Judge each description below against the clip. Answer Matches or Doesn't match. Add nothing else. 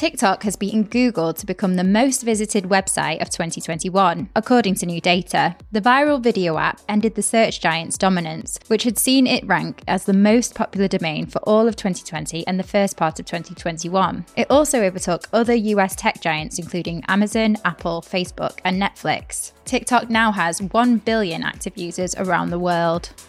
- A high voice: Matches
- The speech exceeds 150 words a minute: Matches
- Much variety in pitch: Doesn't match